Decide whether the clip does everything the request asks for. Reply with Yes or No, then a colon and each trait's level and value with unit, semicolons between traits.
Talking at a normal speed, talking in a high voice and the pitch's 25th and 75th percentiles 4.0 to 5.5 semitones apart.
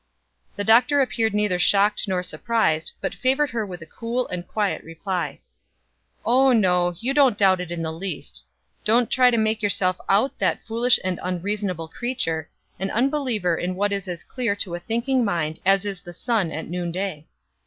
Yes: average, 180 wpm; high, 200 Hz; average, 4.7 semitones